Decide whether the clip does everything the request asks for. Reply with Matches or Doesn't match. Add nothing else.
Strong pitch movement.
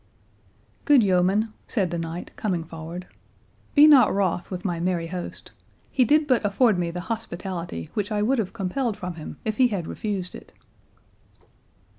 Doesn't match